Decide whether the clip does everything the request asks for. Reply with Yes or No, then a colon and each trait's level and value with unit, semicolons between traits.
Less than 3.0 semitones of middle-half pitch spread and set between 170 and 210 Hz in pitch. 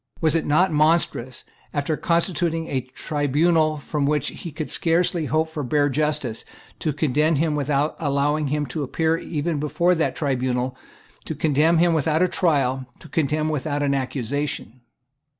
No: narrow, 2.4 semitones; medium, 150 Hz